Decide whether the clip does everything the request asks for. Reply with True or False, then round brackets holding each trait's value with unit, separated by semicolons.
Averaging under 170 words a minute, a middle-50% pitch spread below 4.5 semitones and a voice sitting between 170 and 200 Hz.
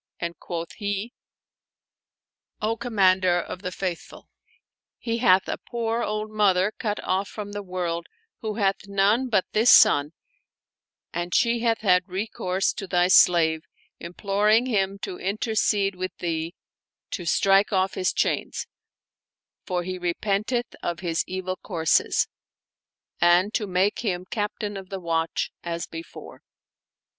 True (140 wpm; 3.0 semitones; 190 Hz)